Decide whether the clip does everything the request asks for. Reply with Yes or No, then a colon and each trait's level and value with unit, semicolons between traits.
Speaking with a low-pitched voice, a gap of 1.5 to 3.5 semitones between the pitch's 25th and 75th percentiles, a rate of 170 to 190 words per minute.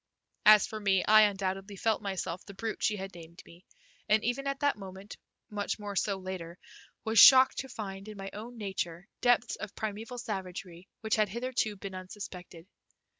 No: high, 205 Hz; narrow, 2.5 semitones; average, 175 wpm